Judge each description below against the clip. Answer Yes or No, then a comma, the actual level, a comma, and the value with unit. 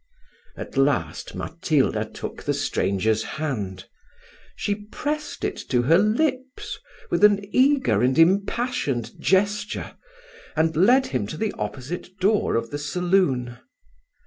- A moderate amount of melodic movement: No, wide, 9.0 semitones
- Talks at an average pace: No, slow, 120 wpm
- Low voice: No, medium, 175 Hz